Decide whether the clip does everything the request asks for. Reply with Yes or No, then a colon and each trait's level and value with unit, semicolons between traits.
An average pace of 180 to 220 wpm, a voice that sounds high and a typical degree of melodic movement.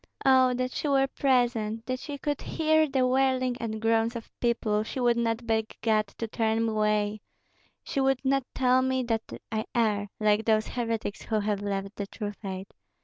Yes: average, 190 wpm; high, 230 Hz; average, 3.1 semitones